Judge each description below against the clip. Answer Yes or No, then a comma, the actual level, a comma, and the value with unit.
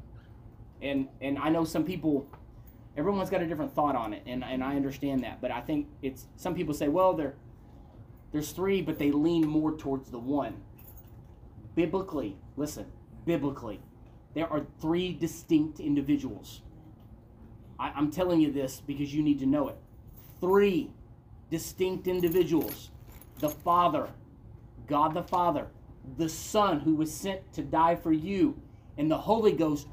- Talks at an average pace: Yes, average, 150 wpm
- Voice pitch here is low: No, medium, 145 Hz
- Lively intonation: Yes, wide, 5.8 semitones